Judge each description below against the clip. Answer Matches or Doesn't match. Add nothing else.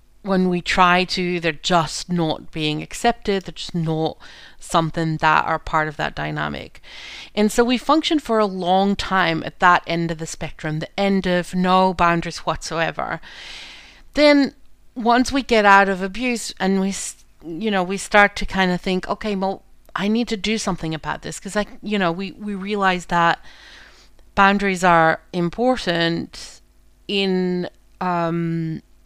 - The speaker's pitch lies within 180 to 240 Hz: Matches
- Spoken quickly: Doesn't match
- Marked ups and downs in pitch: Doesn't match